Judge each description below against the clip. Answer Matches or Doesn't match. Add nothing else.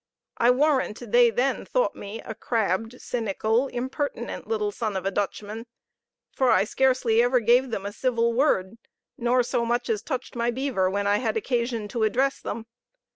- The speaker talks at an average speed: Matches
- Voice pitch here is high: Matches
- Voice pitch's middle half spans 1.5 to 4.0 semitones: Matches